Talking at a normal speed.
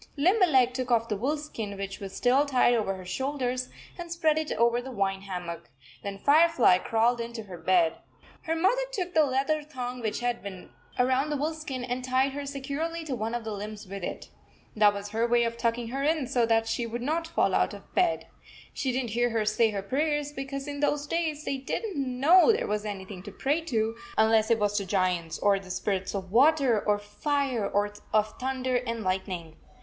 No: fast, 220 wpm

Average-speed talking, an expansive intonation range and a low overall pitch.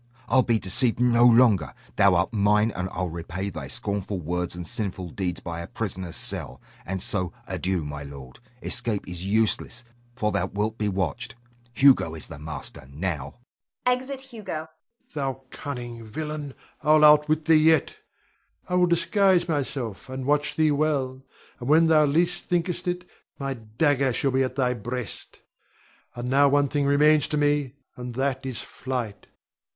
Yes: average, 165 wpm; wide, 7.3 semitones; low, 125 Hz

